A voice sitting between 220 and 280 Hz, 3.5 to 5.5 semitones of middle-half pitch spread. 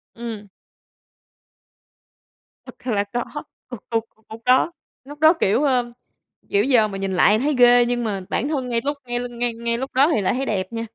No: high, 240 Hz; average, 3.1 semitones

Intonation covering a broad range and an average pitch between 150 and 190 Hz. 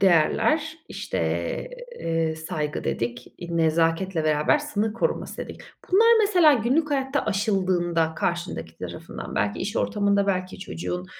Yes: wide, 6.3 semitones; medium, 185 Hz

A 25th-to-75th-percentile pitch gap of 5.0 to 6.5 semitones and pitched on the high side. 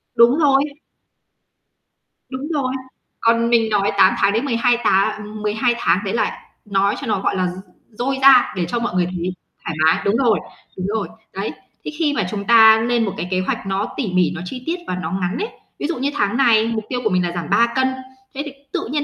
No: average, 4.5 semitones; high, 220 Hz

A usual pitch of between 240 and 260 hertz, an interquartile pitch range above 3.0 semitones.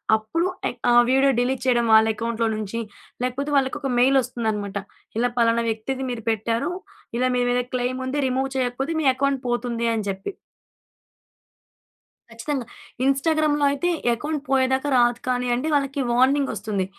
No: very high, 250 Hz; average, 2.7 semitones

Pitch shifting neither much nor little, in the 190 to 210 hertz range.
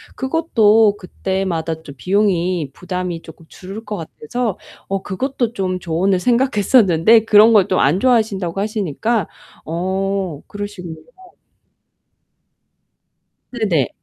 Yes: average, 3.9 semitones; high, 195 Hz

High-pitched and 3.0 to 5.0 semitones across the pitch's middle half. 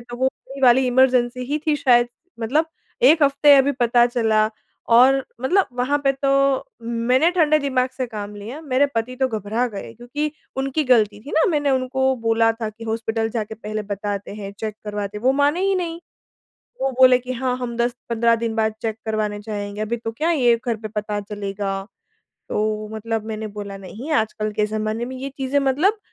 Yes: high, 240 Hz; average, 3.7 semitones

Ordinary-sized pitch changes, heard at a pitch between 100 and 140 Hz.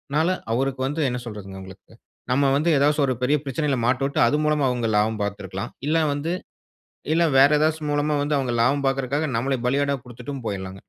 Yes: average, 3.7 semitones; low, 135 Hz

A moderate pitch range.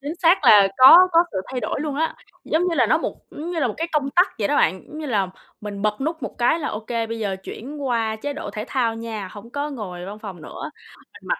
No: wide, 6.3 semitones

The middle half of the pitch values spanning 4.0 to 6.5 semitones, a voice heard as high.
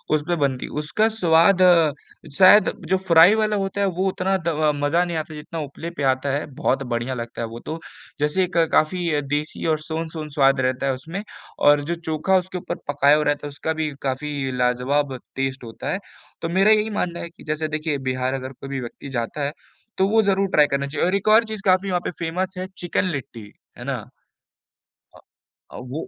No: average, 4.8 semitones; medium, 155 Hz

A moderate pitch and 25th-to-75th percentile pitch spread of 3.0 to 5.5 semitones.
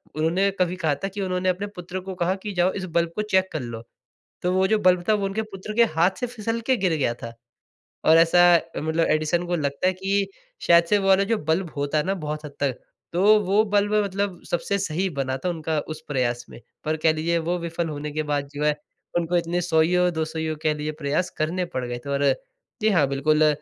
Yes: medium, 170 Hz; average, 3.7 semitones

